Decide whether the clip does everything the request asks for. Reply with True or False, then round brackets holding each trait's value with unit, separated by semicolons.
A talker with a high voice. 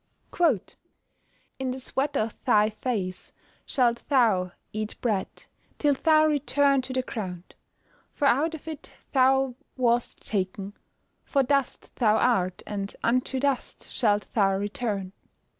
True (245 Hz)